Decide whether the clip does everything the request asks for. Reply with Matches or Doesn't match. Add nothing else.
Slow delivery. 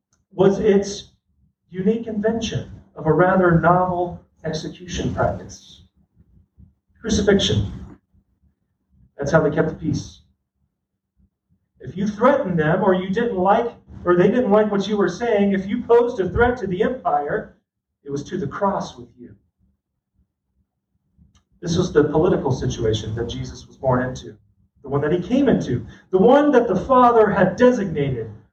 Doesn't match